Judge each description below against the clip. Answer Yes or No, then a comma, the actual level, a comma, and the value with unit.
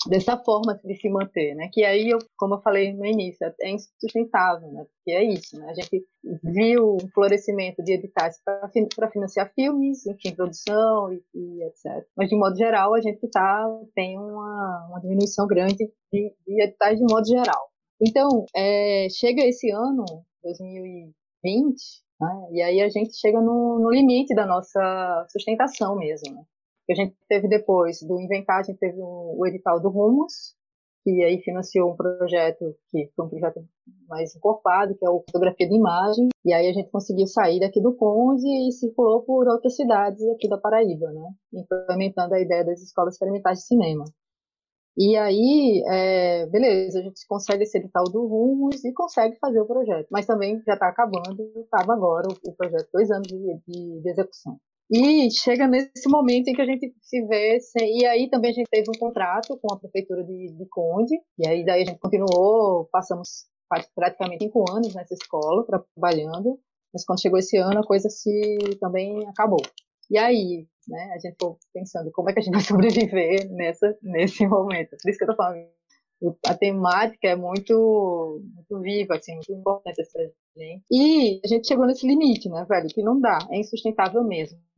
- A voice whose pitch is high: Yes, high, 200 Hz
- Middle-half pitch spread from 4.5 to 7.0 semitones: No, average, 3.6 semitones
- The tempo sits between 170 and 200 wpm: Yes, fast, 185 wpm